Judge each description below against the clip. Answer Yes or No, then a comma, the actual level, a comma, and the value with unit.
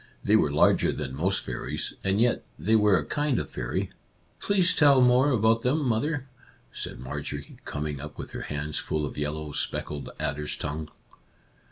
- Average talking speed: Yes, average, 175 wpm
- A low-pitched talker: Yes, very low, 95 Hz